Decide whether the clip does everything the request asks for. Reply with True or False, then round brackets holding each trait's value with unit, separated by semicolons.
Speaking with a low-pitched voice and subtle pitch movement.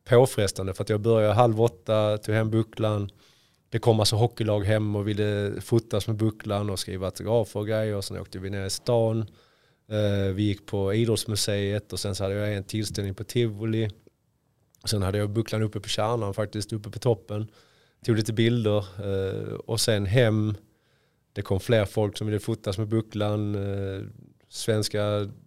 True (105 Hz; 1.8 semitones)